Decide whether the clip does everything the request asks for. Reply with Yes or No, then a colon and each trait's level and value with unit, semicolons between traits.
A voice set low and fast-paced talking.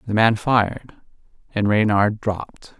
No: low, 110 Hz; slow, 130 wpm